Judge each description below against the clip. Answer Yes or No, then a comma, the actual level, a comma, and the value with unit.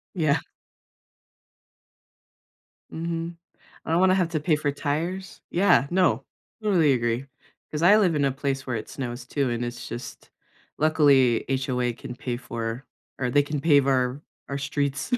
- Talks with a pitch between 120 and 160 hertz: Yes, medium, 140 Hz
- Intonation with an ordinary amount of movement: Yes, average, 4.5 semitones